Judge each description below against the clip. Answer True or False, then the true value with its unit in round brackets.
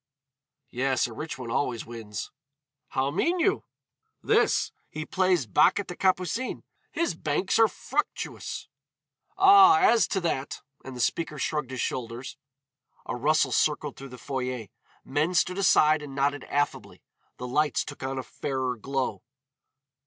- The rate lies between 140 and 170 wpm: True (150 wpm)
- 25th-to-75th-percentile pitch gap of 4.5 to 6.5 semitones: True (5.6 semitones)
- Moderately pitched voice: True (145 Hz)